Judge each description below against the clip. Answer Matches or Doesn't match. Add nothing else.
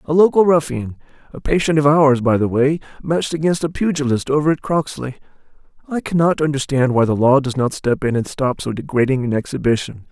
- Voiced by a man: Matches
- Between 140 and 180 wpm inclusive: Doesn't match